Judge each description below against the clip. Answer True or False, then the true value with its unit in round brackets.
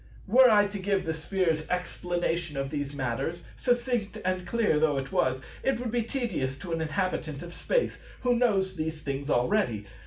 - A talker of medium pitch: True (175 Hz)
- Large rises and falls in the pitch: True (6.1 semitones)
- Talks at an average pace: True (180 wpm)